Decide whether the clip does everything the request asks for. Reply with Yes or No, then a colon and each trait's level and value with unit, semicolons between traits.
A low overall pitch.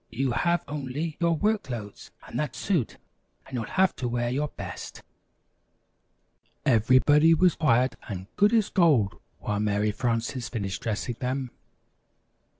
Yes: low, 130 Hz